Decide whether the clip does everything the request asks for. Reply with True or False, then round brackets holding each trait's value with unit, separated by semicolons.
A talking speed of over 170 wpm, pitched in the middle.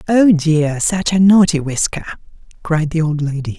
False (165 wpm; 165 Hz)